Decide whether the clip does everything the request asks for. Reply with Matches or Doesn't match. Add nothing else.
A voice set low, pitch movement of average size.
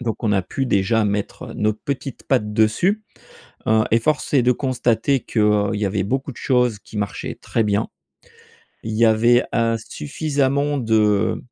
Matches